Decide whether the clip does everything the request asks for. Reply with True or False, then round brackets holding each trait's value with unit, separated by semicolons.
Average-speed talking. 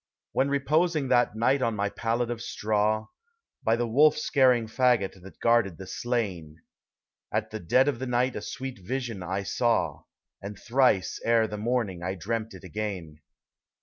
True (165 wpm)